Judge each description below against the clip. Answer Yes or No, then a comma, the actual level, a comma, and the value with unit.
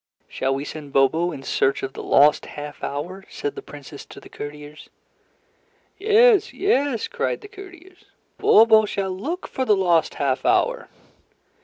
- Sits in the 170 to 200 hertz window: Yes, medium, 185 Hz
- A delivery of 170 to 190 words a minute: No, average, 155 wpm